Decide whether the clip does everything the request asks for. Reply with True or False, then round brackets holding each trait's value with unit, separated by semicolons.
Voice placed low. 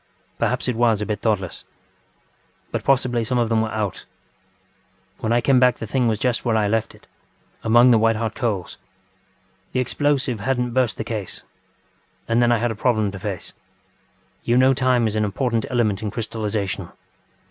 True (115 Hz)